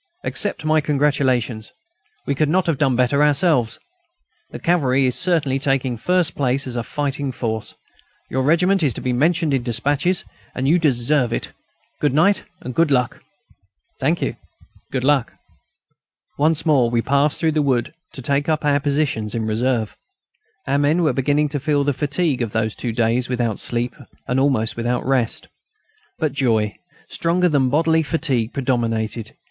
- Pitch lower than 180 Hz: Yes, low, 135 Hz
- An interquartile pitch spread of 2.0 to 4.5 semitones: Yes, average, 3.8 semitones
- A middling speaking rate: Yes, average, 165 wpm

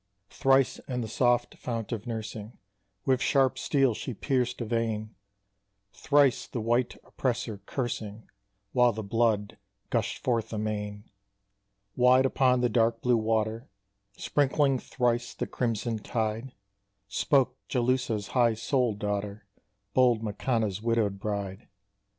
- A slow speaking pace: Yes, slow, 120 wpm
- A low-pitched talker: Yes, low, 115 Hz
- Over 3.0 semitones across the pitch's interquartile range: No, average, 2.7 semitones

